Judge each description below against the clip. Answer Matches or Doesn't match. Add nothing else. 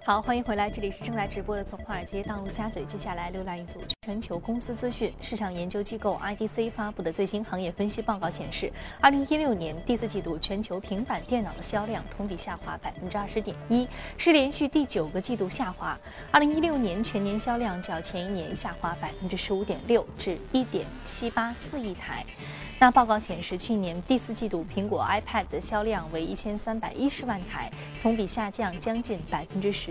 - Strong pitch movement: Doesn't match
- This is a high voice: Matches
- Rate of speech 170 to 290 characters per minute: Matches